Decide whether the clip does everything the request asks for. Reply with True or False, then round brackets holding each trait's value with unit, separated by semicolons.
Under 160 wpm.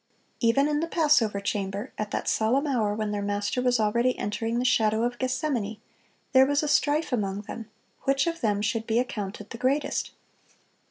False (180 wpm)